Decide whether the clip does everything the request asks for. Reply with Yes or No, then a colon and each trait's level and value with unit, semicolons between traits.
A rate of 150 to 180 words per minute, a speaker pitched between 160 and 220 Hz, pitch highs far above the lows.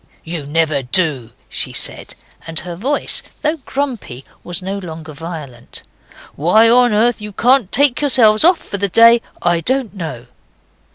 Yes: average, 155 wpm; high, 190 Hz; wide, 7.0 semitones